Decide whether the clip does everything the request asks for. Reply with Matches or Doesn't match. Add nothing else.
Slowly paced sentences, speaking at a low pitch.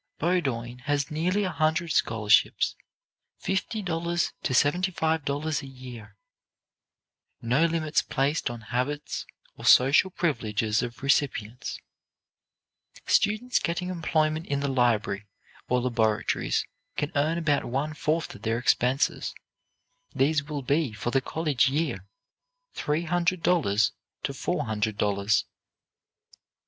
Doesn't match